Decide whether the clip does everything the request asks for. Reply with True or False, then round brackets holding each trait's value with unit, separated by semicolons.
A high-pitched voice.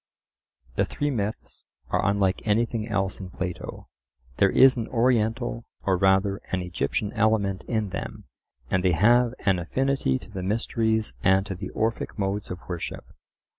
False (100 Hz)